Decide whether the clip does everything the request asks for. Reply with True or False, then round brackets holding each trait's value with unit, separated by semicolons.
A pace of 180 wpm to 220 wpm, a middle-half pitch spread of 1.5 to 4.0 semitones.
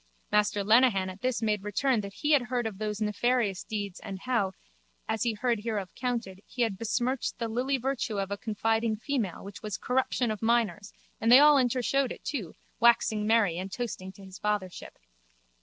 True (190 wpm; 3.4 semitones)